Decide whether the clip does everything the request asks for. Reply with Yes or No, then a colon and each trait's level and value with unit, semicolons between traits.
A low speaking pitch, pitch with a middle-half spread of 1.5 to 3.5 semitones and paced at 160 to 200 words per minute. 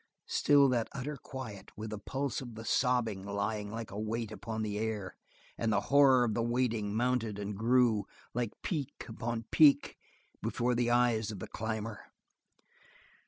Yes: low, 115 Hz; average, 2.7 semitones; average, 165 wpm